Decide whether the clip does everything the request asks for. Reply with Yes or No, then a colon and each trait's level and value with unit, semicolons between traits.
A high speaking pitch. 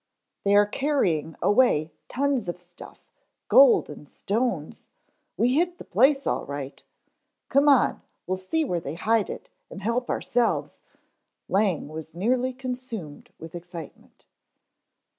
Yes: high, 205 Hz